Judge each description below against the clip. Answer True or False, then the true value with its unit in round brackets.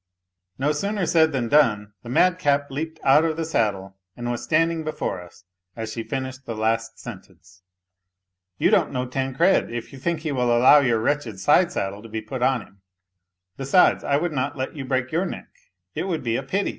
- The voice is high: False (130 Hz)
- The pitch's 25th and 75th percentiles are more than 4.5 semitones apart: True (5.4 semitones)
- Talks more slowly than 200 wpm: False (205 wpm)